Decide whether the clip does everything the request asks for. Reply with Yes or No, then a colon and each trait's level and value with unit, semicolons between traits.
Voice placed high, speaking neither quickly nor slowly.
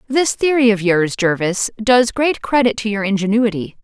Yes: high, 220 Hz; average, 170 wpm